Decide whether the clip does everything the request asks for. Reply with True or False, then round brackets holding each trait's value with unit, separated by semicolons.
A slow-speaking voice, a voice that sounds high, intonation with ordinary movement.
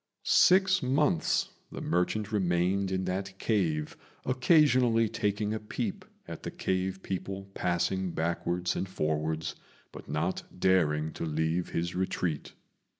False (125 wpm; 95 Hz; 3.6 semitones)